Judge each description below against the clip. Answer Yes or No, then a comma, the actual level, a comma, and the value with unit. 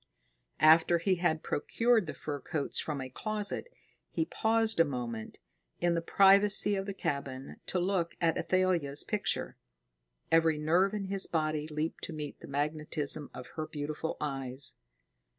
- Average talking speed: Yes, average, 150 wpm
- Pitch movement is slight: No, average, 4.5 semitones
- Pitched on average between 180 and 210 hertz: No, medium, 160 Hz